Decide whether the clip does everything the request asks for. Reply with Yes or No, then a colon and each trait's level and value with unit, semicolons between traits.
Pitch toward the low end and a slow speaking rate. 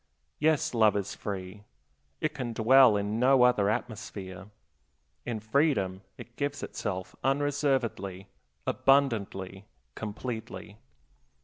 Yes: low, 110 Hz; slow, 100 wpm